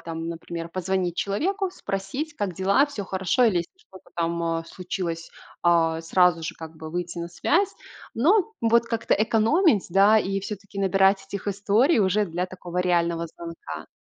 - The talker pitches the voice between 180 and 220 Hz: Yes, high, 190 Hz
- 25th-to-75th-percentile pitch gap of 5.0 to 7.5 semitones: No, average, 4.0 semitones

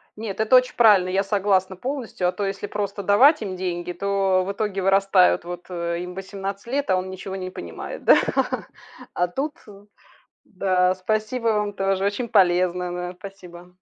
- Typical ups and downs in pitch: No, narrow, 2.3 semitones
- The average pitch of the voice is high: Yes, high, 195 Hz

